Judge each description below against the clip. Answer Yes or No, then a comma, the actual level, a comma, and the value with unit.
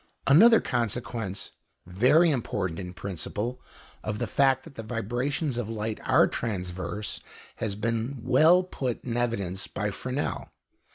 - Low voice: Yes, low, 115 Hz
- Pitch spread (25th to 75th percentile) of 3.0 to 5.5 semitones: Yes, average, 4.4 semitones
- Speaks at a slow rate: Yes, slow, 125 wpm